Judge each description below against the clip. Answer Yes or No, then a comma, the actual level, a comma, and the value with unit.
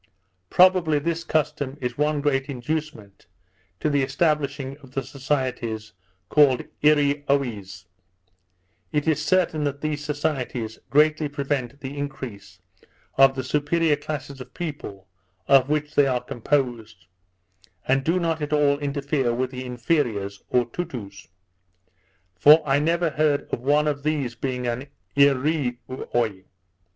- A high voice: No, medium, 140 Hz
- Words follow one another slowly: Yes, slow, 130 wpm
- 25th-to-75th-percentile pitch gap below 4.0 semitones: Yes, average, 3.2 semitones